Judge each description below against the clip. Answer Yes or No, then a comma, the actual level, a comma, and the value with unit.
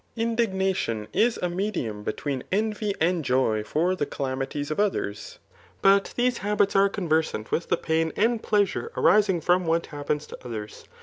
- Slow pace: No, average, 160 wpm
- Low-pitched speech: No, medium, 175 Hz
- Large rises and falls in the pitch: Yes, wide, 6.0 semitones